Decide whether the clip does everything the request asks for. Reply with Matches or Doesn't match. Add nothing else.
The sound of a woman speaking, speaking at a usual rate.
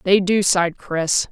Matches